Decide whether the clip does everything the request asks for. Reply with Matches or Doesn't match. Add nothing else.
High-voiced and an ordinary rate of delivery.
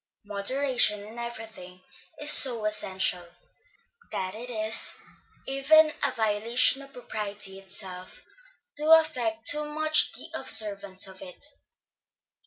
Doesn't match